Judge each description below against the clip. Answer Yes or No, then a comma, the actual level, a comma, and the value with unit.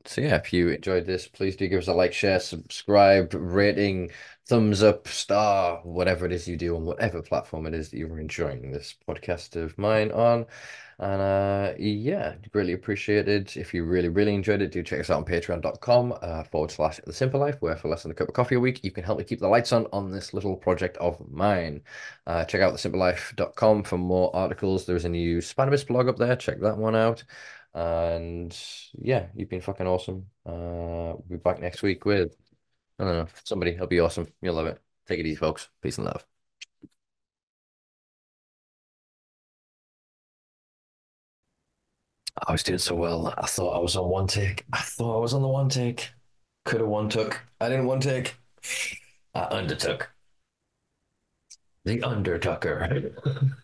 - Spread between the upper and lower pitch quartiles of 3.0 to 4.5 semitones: Yes, average, 3.9 semitones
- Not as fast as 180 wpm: No, average, 185 wpm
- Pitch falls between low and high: No, very low, 95 Hz